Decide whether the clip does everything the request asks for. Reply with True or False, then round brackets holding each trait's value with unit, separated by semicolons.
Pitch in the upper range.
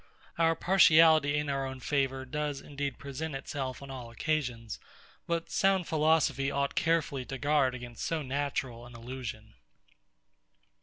False (140 Hz)